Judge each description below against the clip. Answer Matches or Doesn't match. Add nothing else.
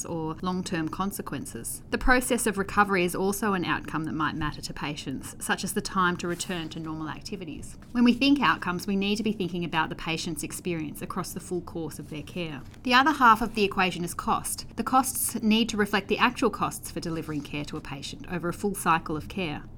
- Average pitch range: Matches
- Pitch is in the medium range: Matches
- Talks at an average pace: Doesn't match